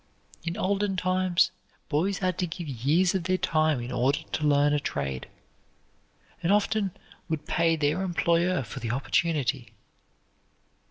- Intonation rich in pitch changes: No, average, 4.4 semitones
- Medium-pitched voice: Yes, medium, 165 Hz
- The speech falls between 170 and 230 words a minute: No, average, 145 wpm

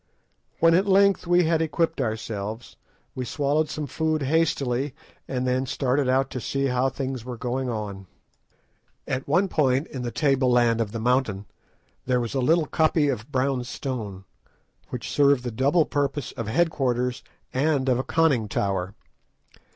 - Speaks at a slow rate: No, average, 165 wpm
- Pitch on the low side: Yes, low, 130 Hz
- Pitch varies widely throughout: No, average, 3.5 semitones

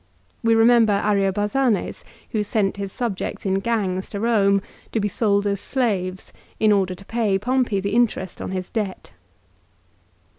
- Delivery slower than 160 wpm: Yes, average, 150 wpm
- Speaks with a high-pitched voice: Yes, high, 205 Hz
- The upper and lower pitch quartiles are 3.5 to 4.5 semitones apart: No, average, 2.7 semitones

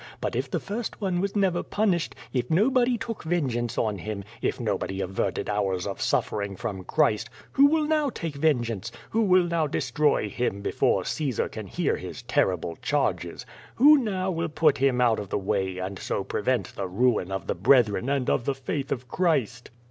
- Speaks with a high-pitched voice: No, low, 130 Hz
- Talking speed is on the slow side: No, average, 185 wpm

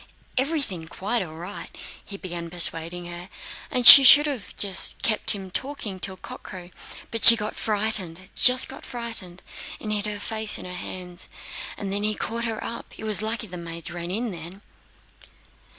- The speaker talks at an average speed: Yes, average, 175 wpm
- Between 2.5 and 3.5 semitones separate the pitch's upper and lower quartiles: No, average, 4.3 semitones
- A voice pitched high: Yes, high, 200 Hz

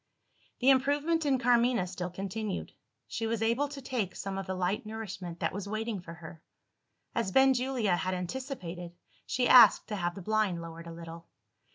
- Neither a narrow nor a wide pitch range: No, wide, 5.7 semitones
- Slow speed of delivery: No, average, 175 wpm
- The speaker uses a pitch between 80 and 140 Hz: No, high, 210 Hz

